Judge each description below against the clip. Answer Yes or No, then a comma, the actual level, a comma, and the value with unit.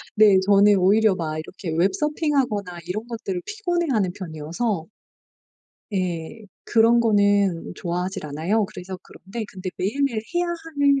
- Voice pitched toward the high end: Yes, high, 200 Hz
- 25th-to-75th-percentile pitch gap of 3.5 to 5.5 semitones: Yes, average, 4.5 semitones